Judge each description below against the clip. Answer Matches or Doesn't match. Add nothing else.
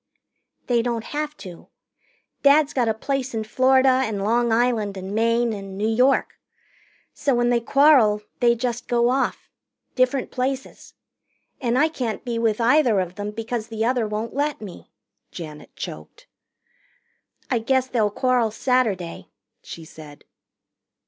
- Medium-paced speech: Matches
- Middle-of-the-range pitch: Doesn't match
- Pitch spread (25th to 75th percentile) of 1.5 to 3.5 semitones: Matches